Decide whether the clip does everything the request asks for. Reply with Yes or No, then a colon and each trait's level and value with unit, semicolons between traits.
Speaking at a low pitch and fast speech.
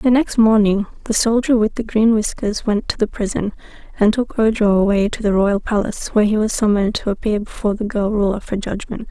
No: high, 210 Hz; fast, 215 wpm